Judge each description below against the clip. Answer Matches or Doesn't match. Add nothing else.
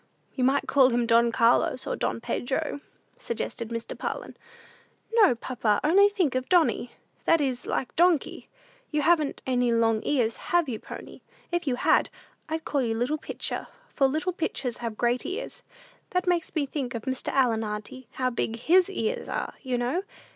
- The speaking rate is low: Doesn't match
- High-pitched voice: Matches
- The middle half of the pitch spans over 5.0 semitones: Matches